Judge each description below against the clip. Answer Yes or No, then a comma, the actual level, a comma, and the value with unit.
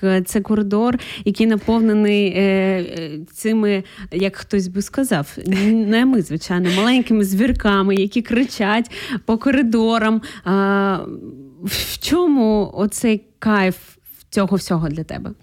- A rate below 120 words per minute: Yes, average, 110 wpm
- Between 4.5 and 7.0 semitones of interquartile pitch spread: No, average, 2.8 semitones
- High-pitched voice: Yes, high, 205 Hz